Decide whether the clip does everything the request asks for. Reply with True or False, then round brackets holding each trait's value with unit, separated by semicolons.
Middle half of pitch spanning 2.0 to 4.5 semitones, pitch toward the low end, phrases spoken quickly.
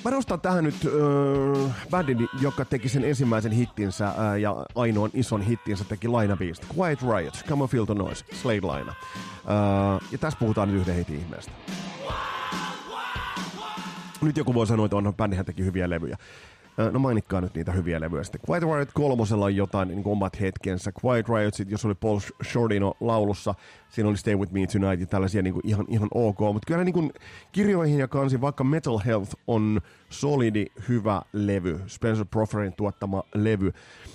False (5.1 semitones; 105 Hz; 170 wpm)